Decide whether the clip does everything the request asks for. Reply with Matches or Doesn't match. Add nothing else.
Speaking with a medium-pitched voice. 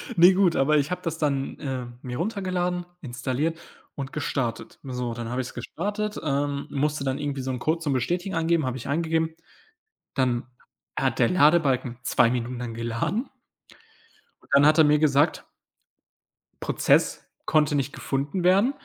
Matches